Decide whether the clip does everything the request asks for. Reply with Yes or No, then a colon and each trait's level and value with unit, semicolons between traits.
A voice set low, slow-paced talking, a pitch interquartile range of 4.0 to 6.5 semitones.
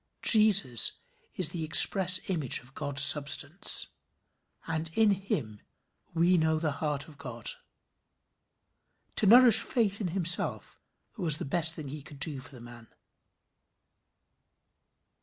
No: medium, 160 Hz; slow, 125 wpm; average, 5.1 semitones